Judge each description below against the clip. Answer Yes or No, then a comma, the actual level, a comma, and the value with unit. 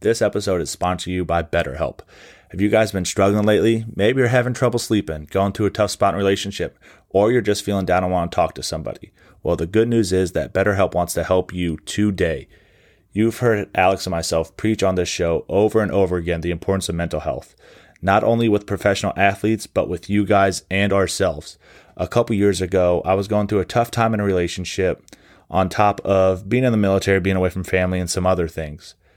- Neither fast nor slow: No, fast, 220 wpm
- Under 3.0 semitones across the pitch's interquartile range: Yes, narrow, 2.5 semitones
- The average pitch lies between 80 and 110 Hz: Yes, very low, 95 Hz